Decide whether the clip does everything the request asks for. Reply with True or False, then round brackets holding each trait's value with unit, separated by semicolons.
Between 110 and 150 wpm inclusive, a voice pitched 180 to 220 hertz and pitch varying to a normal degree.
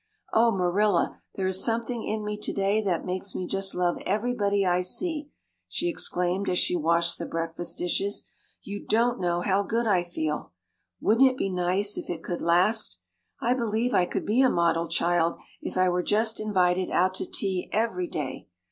False (185 wpm; 190 Hz; 3.6 semitones)